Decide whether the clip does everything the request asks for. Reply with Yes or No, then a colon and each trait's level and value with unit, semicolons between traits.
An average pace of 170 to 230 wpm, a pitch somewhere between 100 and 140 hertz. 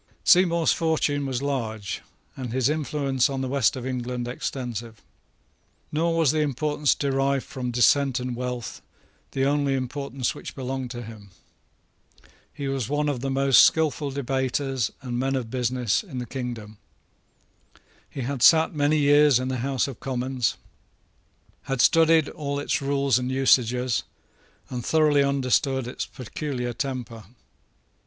No: average, 145 wpm; low, 135 Hz